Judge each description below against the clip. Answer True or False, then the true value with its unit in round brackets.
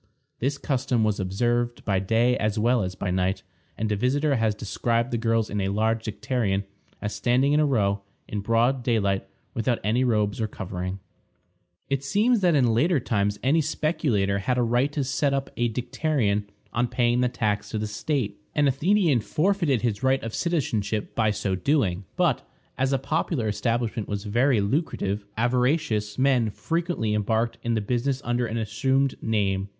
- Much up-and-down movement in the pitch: False (4.3 semitones)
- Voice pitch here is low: True (115 Hz)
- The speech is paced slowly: False (175 wpm)